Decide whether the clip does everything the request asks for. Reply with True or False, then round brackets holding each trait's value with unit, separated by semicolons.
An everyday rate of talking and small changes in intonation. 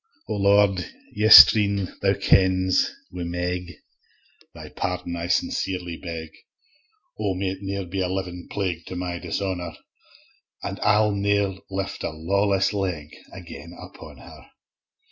False (125 wpm; 2.1 semitones)